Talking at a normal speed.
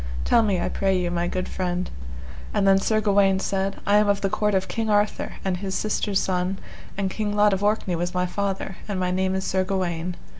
No: fast, 225 wpm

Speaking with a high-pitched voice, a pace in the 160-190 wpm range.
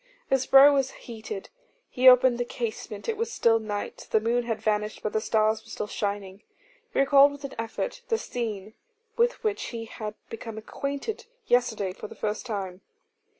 Yes: high, 225 Hz; average, 180 wpm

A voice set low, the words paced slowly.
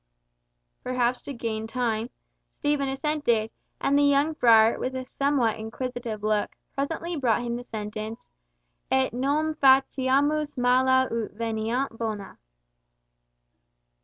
No: very high, 250 Hz; slow, 115 wpm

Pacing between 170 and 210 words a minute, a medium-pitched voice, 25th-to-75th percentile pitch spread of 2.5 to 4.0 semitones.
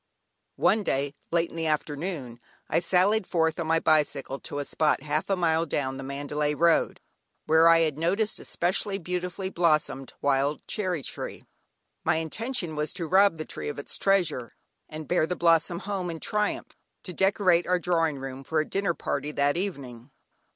Yes: average, 180 wpm; medium, 165 Hz; average, 3.5 semitones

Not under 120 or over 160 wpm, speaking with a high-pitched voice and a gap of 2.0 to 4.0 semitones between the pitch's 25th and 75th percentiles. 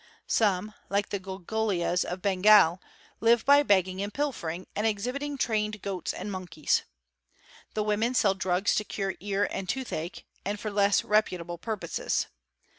Yes: average, 150 wpm; high, 200 Hz; narrow, 2.6 semitones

